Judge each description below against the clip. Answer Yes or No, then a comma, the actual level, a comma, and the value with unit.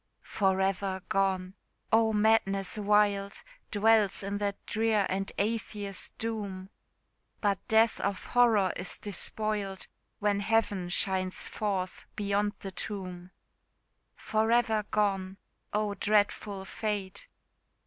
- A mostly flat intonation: Yes, narrow, 1.8 semitones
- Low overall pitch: No, high, 200 Hz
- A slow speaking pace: Yes, slow, 105 wpm